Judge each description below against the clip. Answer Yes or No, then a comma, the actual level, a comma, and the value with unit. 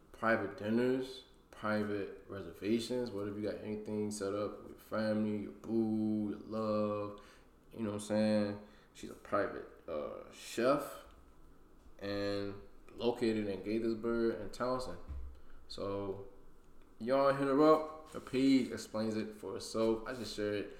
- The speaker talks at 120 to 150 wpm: Yes, slow, 135 wpm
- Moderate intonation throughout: No, narrow, 2.0 semitones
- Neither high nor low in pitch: No, low, 105 Hz